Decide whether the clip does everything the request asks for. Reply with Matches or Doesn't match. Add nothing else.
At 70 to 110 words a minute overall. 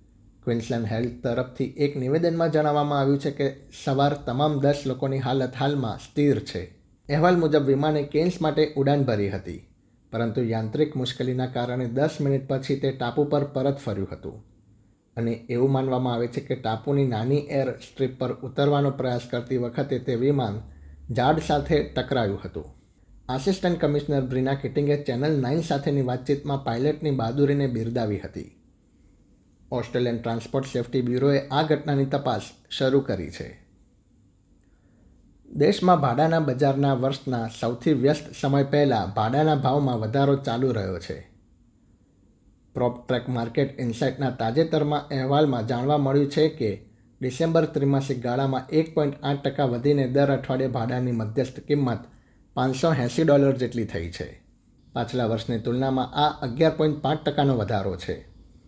Doesn't match